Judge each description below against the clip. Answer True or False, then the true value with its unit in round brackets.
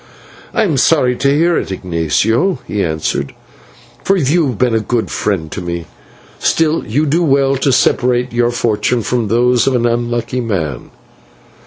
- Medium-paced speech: True (165 wpm)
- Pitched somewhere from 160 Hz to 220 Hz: False (120 Hz)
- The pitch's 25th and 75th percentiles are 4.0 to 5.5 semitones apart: True (4.6 semitones)